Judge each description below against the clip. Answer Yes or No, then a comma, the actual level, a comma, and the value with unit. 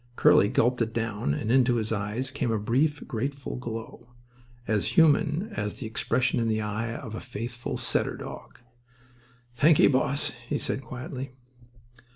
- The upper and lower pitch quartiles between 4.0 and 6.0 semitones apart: No, average, 3.0 semitones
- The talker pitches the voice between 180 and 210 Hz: No, low, 120 Hz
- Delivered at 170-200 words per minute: No, average, 150 wpm